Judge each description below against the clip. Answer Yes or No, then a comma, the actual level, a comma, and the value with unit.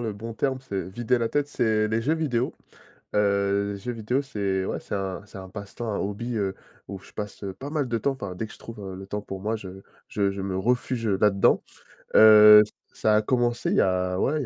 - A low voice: Yes, low, 105 Hz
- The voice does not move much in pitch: No, average, 3.4 semitones